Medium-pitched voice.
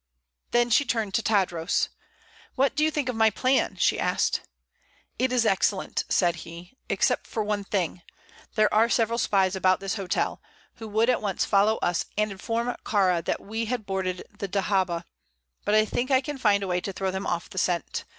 No: high, 205 Hz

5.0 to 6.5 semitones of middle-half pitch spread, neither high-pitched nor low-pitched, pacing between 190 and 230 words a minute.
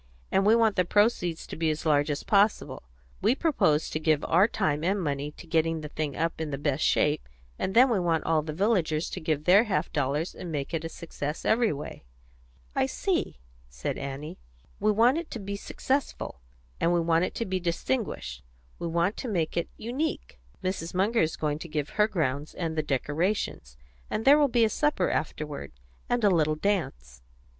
Yes: average, 5.3 semitones; medium, 165 Hz; average, 200 wpm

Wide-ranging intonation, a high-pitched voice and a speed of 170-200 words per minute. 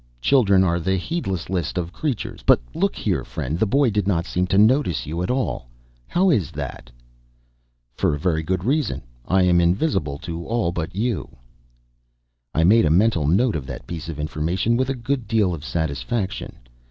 No: wide, 6.1 semitones; very low, 95 Hz; average, 180 wpm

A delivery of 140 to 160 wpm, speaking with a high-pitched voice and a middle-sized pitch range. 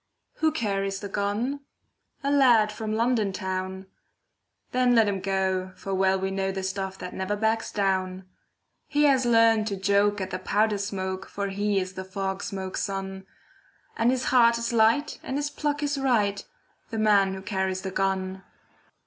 No: average, 175 wpm; high, 200 Hz; average, 3.1 semitones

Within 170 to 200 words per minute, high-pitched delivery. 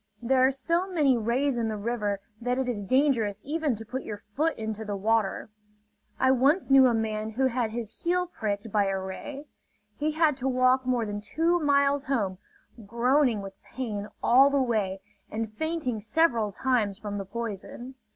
Yes: average, 180 wpm; high, 240 Hz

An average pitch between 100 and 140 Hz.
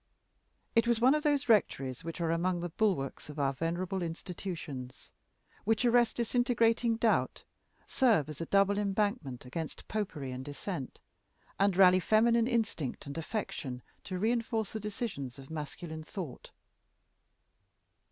No: medium, 185 Hz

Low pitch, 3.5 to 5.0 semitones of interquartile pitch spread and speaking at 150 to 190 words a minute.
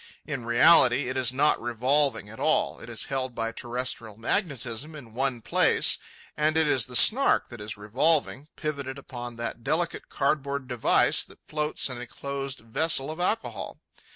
Yes: low, 130 Hz; average, 4.0 semitones; average, 165 wpm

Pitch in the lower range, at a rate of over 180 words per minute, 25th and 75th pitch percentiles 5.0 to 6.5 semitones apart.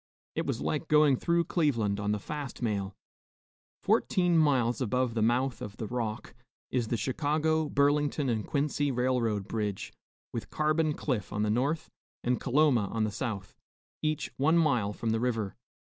No: low, 125 Hz; average, 160 wpm; average, 5.3 semitones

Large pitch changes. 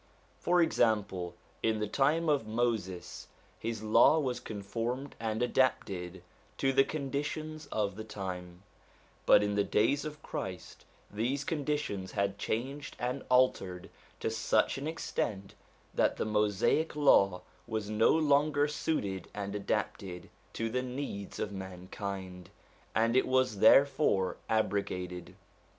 Yes: wide, 5.7 semitones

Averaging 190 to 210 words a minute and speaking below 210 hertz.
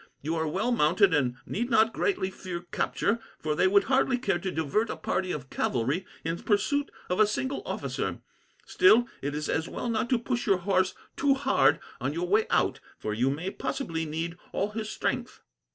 Yes: average, 195 wpm; high, 190 Hz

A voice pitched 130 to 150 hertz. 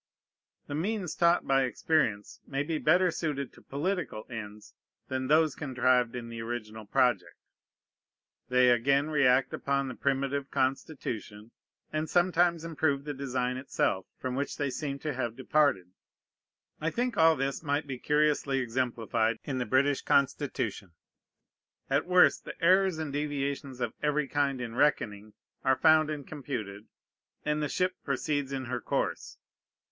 Yes: medium, 140 Hz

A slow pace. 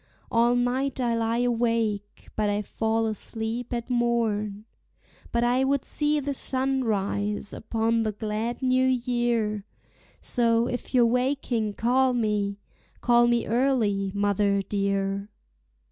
Yes: slow, 130 wpm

